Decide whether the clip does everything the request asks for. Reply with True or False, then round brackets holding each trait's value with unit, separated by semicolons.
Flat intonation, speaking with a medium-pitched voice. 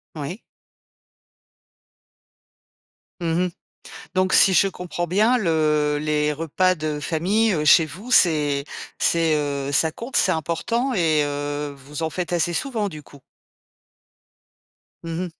False (3.8 semitones; 165 Hz)